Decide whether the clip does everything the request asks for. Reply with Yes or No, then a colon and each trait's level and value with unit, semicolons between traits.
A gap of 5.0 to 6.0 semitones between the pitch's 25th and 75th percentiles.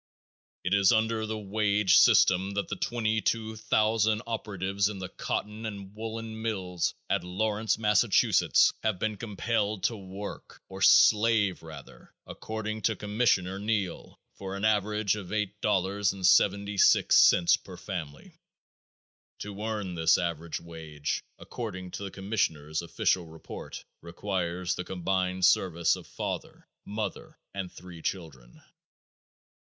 No: average, 3.0 semitones